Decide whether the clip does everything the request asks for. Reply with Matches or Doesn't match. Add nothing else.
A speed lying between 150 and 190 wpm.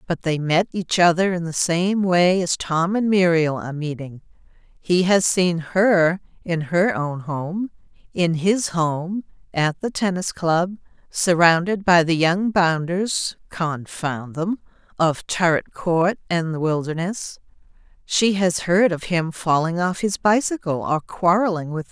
Matches